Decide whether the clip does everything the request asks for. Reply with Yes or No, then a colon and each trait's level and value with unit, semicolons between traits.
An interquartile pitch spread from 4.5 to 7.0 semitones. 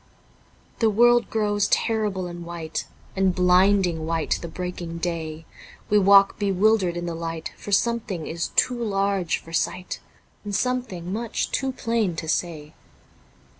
No: average, 3.8 semitones